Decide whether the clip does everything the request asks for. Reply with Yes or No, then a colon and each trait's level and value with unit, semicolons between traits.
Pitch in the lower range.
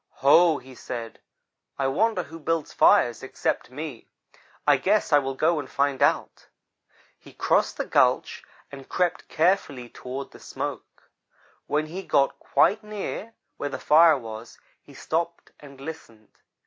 No: medium, 145 Hz